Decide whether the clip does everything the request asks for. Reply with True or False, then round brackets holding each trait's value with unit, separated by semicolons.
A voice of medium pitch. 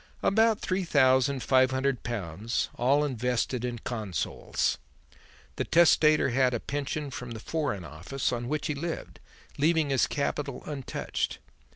False (130 Hz)